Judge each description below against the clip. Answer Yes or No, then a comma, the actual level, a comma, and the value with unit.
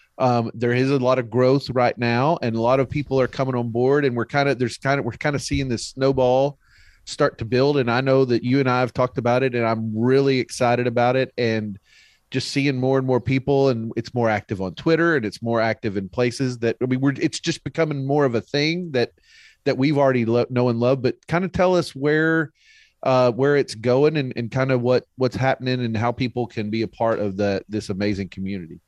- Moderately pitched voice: No, low, 125 Hz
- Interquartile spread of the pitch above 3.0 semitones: No, average, 2.7 semitones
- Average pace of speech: No, fast, 245 wpm